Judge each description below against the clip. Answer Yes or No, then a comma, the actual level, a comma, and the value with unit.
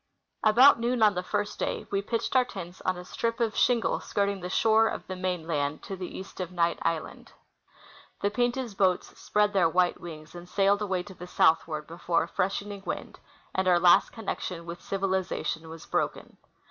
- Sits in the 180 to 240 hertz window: Yes, high, 190 Hz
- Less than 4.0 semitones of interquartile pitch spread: Yes, average, 3.1 semitones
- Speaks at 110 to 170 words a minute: No, average, 185 wpm